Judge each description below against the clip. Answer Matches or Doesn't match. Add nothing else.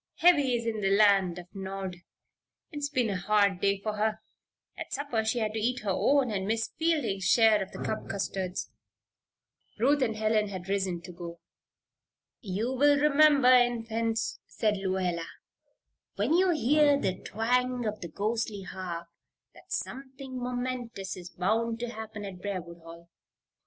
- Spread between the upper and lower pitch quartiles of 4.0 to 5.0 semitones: Matches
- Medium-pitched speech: Doesn't match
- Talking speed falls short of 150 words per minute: Doesn't match